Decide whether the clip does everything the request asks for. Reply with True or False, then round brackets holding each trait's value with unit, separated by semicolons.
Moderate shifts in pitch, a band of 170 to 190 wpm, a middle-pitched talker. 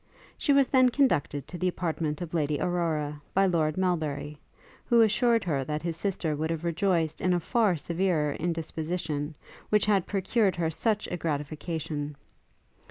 False (3.9 semitones; 160 wpm; 170 Hz)